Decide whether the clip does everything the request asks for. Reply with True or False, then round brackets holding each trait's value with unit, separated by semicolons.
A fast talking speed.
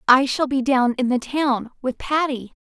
False (180 wpm)